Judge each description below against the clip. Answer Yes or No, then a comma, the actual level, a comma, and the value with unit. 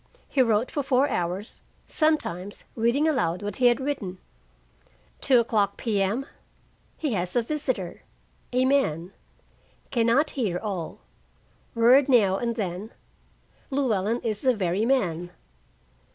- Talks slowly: Yes, slow, 125 wpm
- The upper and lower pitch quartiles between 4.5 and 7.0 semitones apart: Yes, wide, 5.4 semitones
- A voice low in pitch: No, high, 230 Hz